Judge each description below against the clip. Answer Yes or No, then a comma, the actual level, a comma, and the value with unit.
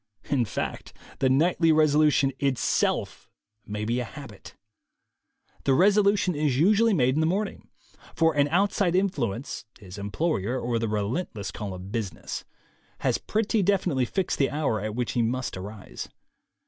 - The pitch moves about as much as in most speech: No, wide, 7.6 semitones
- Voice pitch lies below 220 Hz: Yes, medium, 140 Hz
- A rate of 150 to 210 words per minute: Yes, average, 155 wpm